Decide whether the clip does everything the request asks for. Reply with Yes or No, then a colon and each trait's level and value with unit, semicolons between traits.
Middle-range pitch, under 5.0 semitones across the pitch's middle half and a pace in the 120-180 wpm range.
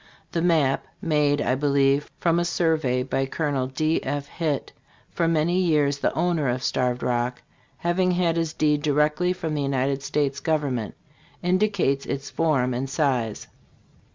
Yes: medium, 145 Hz; average, 3.5 semitones; average, 155 wpm